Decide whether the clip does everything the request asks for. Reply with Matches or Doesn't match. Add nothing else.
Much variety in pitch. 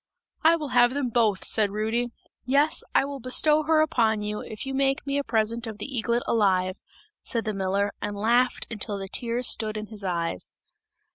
Doesn't match